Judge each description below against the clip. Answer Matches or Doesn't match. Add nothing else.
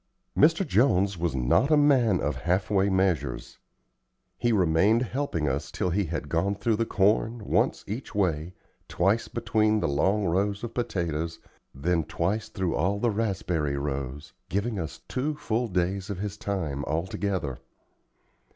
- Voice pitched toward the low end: Matches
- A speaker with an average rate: Matches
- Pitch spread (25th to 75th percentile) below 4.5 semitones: Doesn't match